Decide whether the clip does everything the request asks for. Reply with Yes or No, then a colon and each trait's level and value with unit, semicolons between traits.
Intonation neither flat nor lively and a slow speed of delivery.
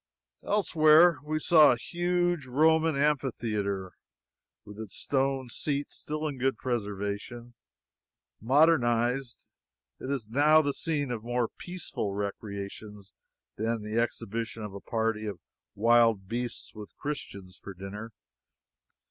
No: wide, 5.7 semitones; slow, 120 wpm